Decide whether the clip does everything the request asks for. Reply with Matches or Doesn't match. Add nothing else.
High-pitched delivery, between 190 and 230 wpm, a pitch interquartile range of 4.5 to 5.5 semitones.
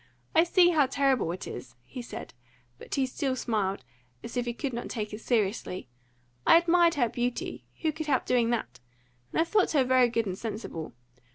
Matches